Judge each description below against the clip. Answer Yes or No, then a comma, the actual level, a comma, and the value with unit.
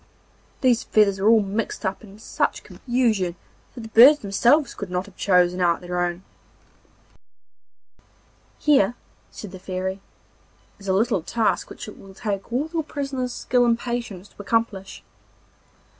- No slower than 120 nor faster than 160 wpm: Yes, average, 150 wpm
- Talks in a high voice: Yes, high, 210 Hz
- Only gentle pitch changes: No, average, 4.1 semitones